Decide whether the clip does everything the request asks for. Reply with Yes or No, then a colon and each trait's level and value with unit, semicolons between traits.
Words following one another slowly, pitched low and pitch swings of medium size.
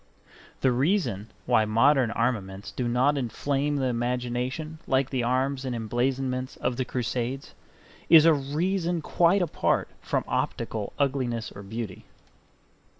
Yes: slow, 130 wpm; low, 130 Hz; average, 3.2 semitones